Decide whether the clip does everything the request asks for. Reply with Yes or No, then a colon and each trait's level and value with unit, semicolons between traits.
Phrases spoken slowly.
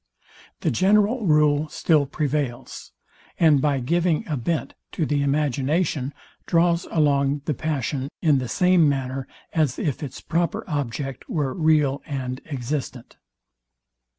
Yes: slow, 125 wpm